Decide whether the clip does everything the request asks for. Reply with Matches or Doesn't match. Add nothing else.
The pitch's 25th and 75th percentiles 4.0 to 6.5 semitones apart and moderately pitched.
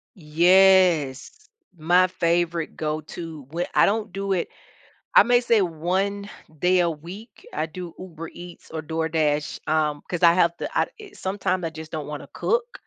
Doesn't match